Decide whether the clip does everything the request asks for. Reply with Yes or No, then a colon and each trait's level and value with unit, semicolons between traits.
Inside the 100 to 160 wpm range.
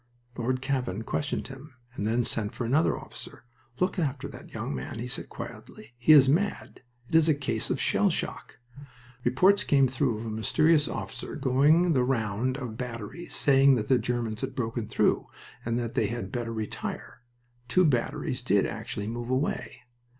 No: average, 180 wpm